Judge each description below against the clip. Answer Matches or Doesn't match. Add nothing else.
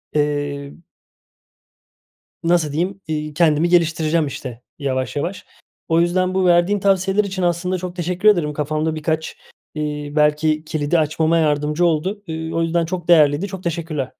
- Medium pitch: Matches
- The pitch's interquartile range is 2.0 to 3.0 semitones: Matches